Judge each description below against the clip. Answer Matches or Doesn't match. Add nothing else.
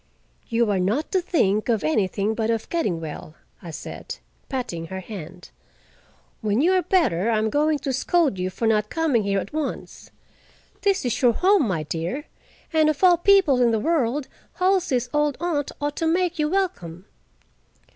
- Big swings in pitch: Matches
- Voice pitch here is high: Matches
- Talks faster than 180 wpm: Doesn't match